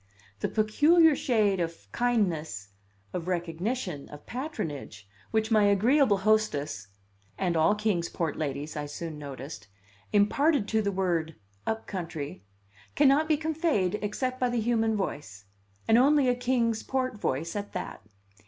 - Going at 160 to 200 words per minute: No, average, 140 wpm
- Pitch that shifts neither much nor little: No, wide, 7.2 semitones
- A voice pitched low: No, high, 205 Hz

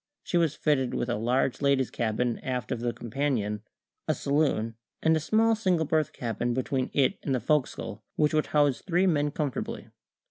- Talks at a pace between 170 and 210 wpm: Yes, average, 180 wpm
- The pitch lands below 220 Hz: Yes, medium, 140 Hz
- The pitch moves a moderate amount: Yes, average, 4.2 semitones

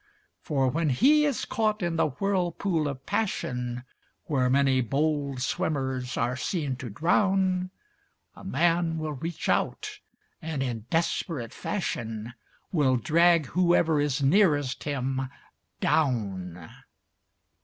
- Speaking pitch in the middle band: Yes, medium, 145 Hz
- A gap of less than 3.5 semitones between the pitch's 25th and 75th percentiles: No, average, 5.1 semitones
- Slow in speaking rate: Yes, slow, 115 wpm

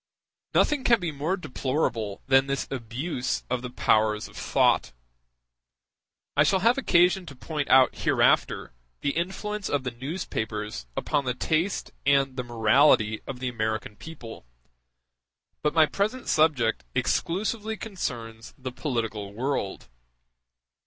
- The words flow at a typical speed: No, slow, 130 wpm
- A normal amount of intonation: No, wide, 6.3 semitones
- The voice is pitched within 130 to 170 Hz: Yes, low, 135 Hz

